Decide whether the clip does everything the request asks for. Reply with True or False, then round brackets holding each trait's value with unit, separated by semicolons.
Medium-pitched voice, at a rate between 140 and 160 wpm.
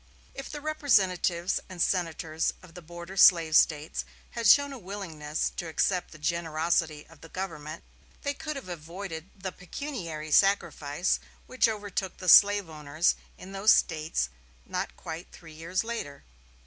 True (175 Hz; 150 wpm)